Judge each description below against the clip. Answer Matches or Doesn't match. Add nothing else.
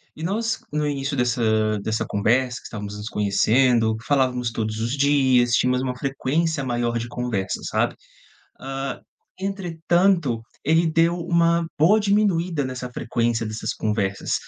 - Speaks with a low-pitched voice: Matches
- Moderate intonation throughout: Doesn't match